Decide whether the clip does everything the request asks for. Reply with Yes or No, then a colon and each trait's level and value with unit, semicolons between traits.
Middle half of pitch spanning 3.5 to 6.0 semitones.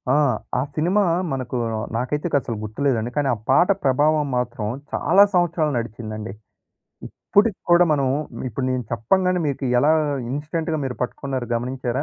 Yes: average, 4.4 semitones